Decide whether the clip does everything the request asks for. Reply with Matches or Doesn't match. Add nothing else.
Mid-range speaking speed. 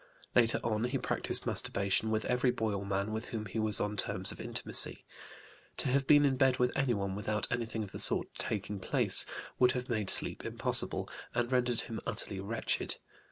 Matches